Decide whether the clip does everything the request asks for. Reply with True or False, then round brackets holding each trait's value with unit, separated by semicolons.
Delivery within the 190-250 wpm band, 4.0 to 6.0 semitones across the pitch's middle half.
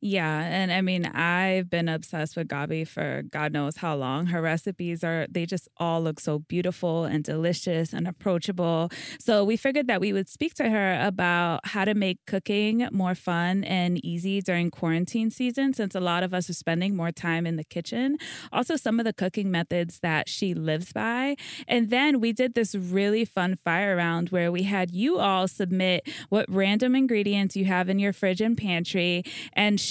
False (195 wpm; 3.2 semitones)